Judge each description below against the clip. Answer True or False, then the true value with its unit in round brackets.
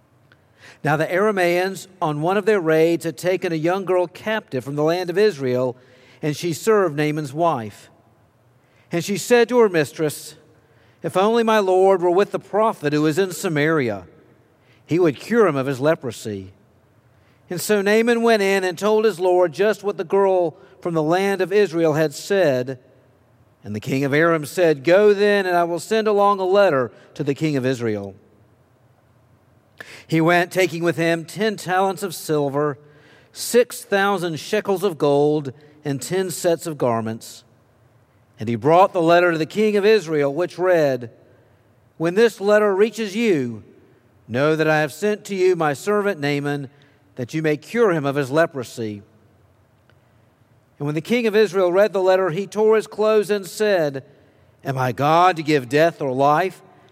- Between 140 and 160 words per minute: False (175 wpm)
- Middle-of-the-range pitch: True (160 Hz)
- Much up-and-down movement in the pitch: True (6.9 semitones)